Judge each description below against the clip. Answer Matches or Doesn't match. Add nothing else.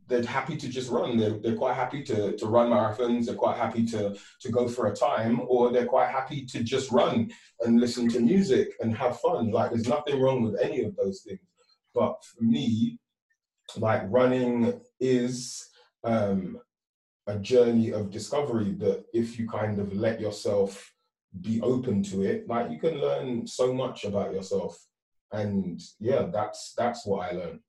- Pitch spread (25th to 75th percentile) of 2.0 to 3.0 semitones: Matches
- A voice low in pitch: Matches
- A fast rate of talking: Doesn't match